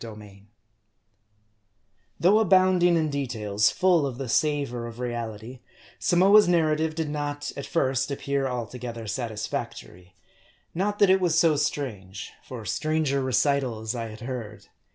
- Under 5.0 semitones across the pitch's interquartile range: No, wide, 5.5 semitones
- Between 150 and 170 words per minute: No, slow, 135 wpm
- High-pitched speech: No, low, 135 Hz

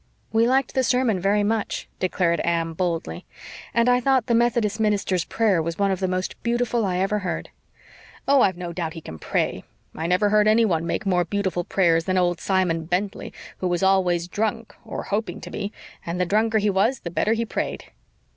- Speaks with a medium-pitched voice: No, high, 195 Hz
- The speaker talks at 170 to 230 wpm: Yes, average, 200 wpm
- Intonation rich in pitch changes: No, average, 4.0 semitones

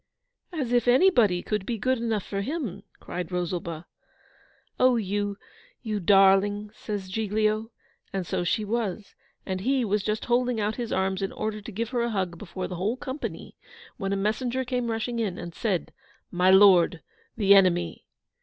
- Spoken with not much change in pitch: No, average, 3.6 semitones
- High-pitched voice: Yes, high, 210 Hz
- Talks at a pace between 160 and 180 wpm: Yes, average, 170 wpm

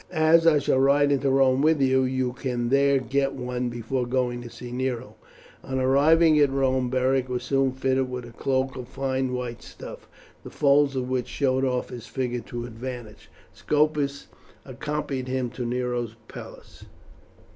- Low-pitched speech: Yes, low, 130 Hz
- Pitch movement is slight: Yes, narrow, 1.7 semitones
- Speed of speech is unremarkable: Yes, average, 165 wpm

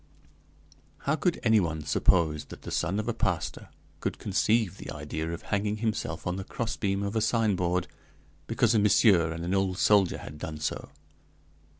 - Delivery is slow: No, average, 175 wpm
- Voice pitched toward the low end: Yes, very low, 95 Hz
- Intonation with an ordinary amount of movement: Yes, average, 4.2 semitones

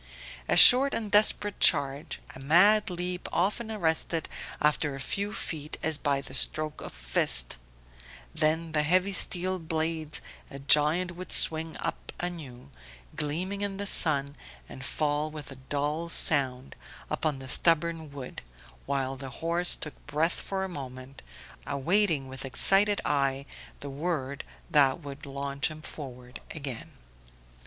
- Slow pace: No, average, 145 wpm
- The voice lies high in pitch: No, medium, 155 Hz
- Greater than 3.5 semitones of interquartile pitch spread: Yes, average, 4.2 semitones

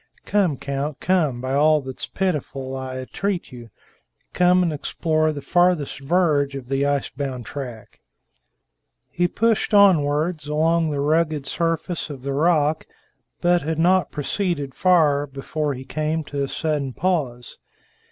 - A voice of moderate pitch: Yes, medium, 150 Hz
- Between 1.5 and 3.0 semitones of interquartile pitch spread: No, average, 3.8 semitones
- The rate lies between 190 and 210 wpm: No, average, 145 wpm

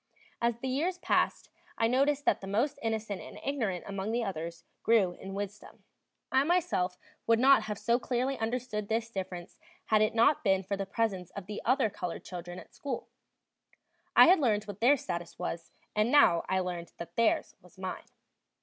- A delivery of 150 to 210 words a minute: Yes, average, 185 wpm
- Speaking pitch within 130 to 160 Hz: No, high, 215 Hz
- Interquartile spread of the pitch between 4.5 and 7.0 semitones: Yes, average, 4.9 semitones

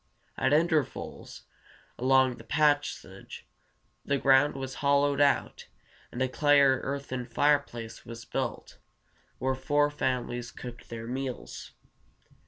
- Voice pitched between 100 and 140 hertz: Yes, low, 135 Hz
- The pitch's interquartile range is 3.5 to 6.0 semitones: No, narrow, 2.5 semitones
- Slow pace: Yes, slow, 115 wpm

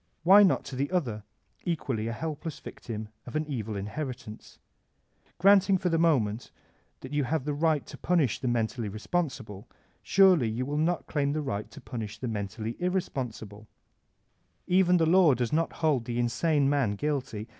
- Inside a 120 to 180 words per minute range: No, average, 190 wpm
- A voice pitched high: No, low, 135 Hz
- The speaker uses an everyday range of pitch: No, wide, 6.5 semitones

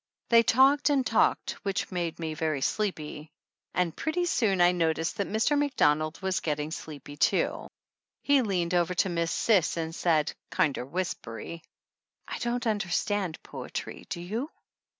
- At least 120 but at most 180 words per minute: Yes, average, 150 wpm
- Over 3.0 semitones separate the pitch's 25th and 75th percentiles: Yes, wide, 5.4 semitones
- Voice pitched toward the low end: No, medium, 180 Hz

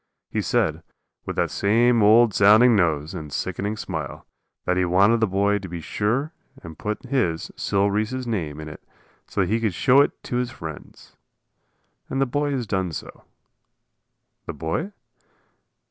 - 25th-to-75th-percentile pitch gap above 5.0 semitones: Yes, wide, 5.6 semitones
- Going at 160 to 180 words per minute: Yes, average, 165 wpm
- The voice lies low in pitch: Yes, low, 105 Hz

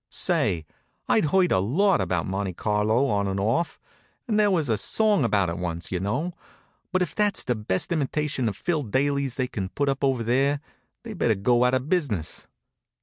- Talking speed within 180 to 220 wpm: Yes, average, 190 wpm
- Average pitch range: No, wide, 7.2 semitones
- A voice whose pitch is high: No, low, 125 Hz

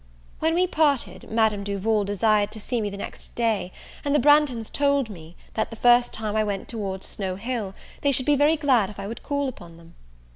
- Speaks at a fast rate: Yes, fast, 215 wpm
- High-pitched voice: Yes, high, 220 Hz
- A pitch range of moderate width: No, wide, 5.7 semitones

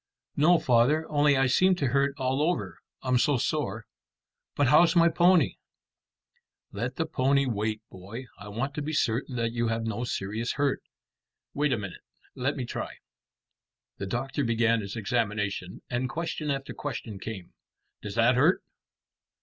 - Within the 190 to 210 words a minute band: No, average, 160 wpm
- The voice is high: No, low, 125 Hz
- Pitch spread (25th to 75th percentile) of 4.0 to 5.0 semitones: Yes, average, 4.4 semitones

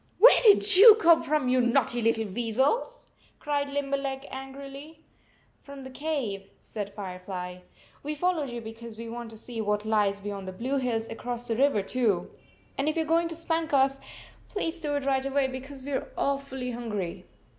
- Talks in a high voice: Yes, very high, 265 Hz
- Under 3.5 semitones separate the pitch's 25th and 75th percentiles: No, average, 4.3 semitones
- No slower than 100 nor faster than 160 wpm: No, average, 185 wpm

